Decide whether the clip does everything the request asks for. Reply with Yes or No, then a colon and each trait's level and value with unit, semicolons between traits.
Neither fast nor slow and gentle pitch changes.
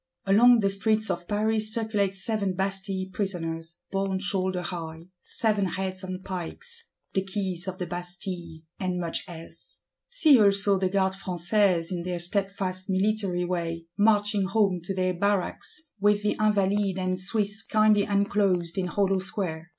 Yes: average, 150 wpm; narrow, 2.3 semitones